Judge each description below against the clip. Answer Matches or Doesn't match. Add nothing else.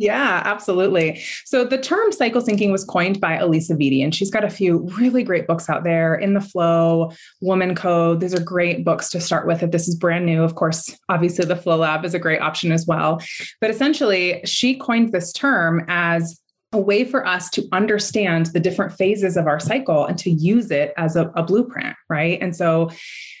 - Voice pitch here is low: Doesn't match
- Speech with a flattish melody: Doesn't match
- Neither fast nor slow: Doesn't match